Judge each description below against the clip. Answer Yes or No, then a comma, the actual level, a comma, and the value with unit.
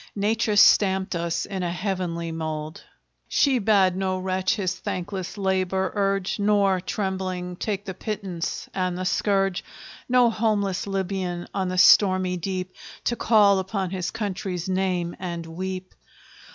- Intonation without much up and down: Yes, narrow, 1.7 semitones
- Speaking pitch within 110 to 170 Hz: No, high, 190 Hz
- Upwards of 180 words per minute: No, average, 140 wpm